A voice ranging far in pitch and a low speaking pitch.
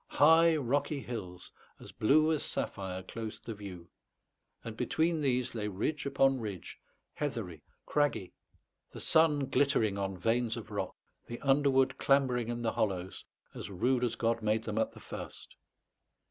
No: average, 5.0 semitones; low, 120 Hz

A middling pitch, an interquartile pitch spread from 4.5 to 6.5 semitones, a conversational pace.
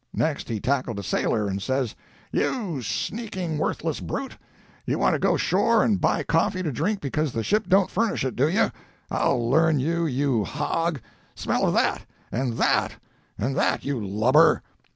Yes: medium, 145 Hz; wide, 5.6 semitones; average, 165 wpm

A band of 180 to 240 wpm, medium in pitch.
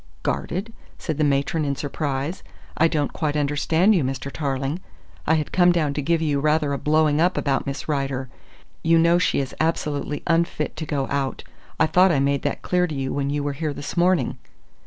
Yes: average, 200 wpm; medium, 150 Hz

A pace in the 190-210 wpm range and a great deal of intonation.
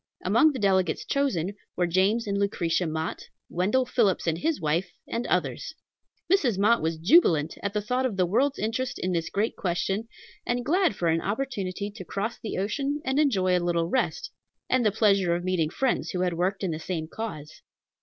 Yes: average, 195 wpm; wide, 5.7 semitones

